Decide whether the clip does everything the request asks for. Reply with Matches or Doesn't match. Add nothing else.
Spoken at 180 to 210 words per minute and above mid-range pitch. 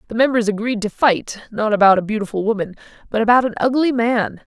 Matches